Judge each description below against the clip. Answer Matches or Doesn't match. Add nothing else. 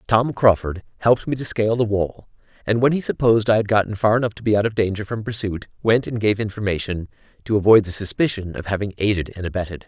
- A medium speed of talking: Doesn't match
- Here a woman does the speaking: Doesn't match